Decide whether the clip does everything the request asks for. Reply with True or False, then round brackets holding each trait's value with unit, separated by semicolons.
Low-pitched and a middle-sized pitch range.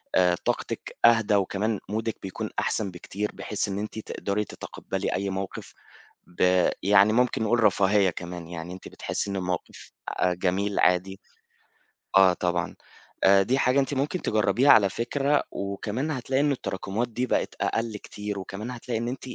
True (105 Hz; 3.7 semitones)